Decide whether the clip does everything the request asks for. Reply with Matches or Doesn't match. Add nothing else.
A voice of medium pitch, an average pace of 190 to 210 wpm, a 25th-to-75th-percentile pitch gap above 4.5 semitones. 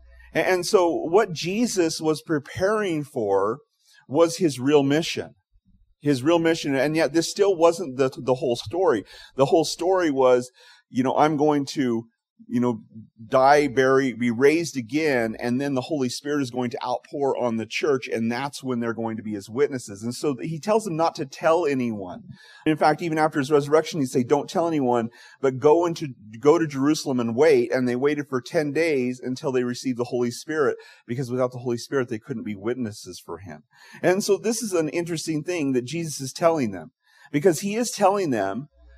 Matches